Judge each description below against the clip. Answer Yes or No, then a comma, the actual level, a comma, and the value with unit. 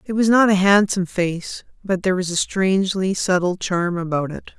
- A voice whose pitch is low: No, medium, 185 Hz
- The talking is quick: No, average, 195 wpm